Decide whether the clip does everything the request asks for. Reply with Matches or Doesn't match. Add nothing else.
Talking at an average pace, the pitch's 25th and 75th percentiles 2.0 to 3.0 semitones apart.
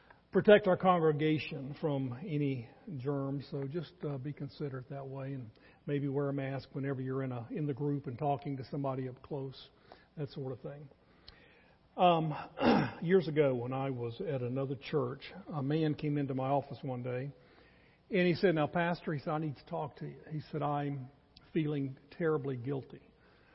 Matches